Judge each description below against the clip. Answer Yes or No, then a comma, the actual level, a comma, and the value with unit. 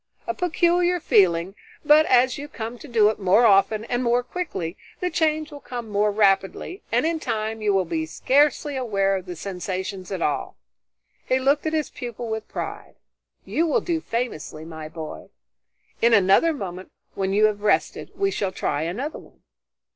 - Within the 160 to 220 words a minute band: Yes, average, 175 wpm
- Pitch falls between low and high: No, high, 220 Hz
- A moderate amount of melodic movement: No, wide, 7.2 semitones